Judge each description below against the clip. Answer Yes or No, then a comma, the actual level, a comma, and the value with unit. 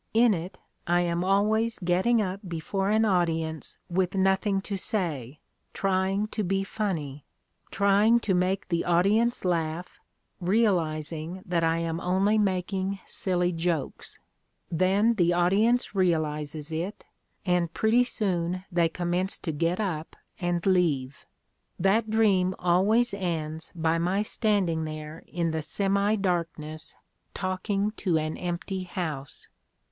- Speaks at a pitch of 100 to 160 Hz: No, medium, 180 Hz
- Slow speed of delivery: Yes, slow, 130 wpm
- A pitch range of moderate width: Yes, average, 3.1 semitones